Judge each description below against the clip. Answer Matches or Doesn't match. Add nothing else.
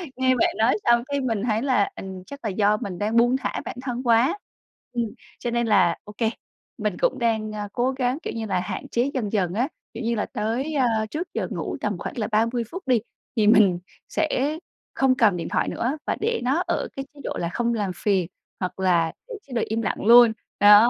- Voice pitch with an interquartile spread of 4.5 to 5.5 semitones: Doesn't match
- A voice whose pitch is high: Matches